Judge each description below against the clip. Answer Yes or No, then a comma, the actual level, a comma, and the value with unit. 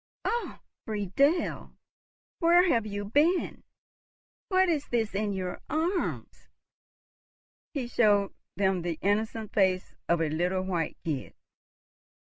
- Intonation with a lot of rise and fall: Yes, wide, 7.7 semitones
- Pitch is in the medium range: No, high, 205 Hz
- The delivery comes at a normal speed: No, slow, 115 wpm